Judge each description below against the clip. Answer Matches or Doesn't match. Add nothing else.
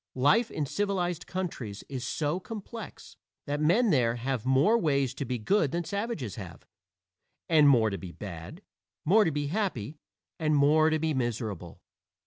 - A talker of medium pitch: Matches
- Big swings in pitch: Matches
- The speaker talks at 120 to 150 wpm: Doesn't match